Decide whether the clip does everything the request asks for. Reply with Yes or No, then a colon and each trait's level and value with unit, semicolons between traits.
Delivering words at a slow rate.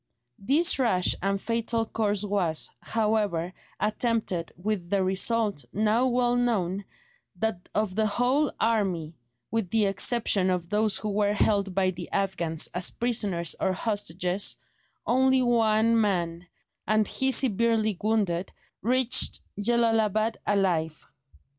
Yes: slow, 120 wpm